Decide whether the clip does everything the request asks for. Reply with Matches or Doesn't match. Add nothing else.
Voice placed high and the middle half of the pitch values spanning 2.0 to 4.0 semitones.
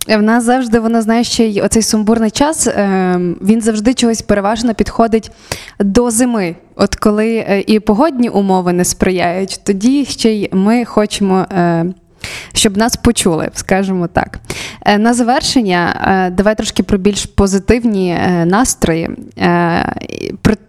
Matches